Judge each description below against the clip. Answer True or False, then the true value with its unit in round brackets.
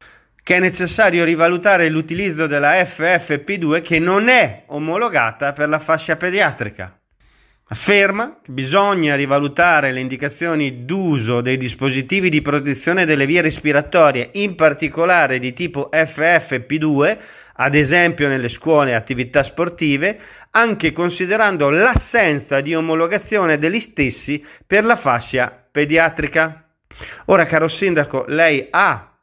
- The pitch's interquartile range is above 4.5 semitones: False (3.8 semitones)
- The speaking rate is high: False (115 wpm)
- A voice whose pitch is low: False (160 Hz)